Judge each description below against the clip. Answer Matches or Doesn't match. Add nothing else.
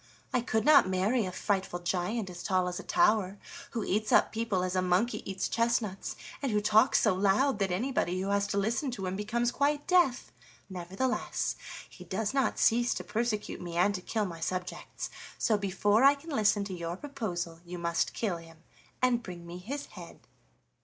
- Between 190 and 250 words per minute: Matches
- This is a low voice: Doesn't match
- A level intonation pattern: Doesn't match